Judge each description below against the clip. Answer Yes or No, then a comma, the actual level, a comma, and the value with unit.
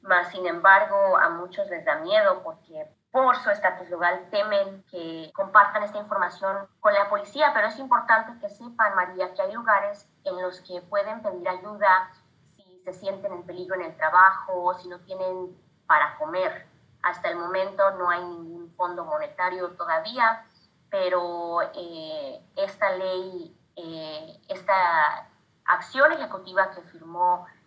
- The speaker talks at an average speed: Yes, average, 145 wpm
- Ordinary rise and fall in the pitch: Yes, average, 4.0 semitones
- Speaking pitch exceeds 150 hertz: Yes, high, 190 Hz